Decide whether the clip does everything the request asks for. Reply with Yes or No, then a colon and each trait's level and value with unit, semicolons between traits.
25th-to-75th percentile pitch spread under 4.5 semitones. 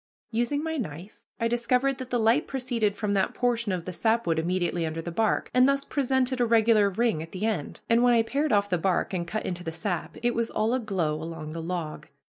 No: wide, 5.5 semitones